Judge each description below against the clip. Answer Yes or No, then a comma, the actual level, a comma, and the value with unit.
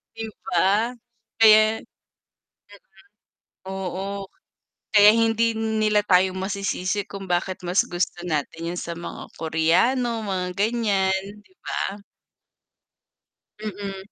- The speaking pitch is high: Yes, high, 195 Hz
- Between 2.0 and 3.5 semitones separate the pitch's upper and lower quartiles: Yes, average, 3.1 semitones